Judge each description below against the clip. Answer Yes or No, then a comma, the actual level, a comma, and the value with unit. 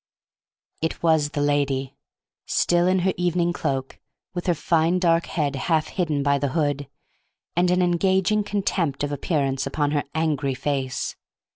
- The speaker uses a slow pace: No, average, 150 wpm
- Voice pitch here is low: No, medium, 155 Hz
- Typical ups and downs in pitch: Yes, average, 3.7 semitones